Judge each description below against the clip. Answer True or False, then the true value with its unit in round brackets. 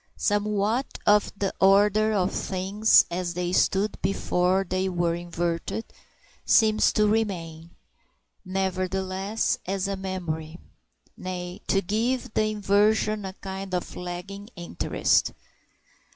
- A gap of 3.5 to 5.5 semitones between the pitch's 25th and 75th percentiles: False (2.6 semitones)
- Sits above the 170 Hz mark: True (190 Hz)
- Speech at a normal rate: False (110 wpm)